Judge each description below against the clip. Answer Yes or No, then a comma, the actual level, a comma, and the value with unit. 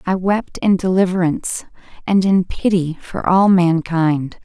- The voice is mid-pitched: Yes, medium, 180 Hz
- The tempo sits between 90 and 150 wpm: Yes, slow, 135 wpm